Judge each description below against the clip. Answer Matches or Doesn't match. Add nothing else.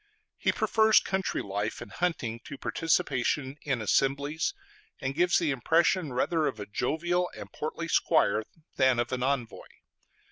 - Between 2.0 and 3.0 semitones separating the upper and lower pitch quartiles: Doesn't match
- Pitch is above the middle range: Doesn't match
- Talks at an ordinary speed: Matches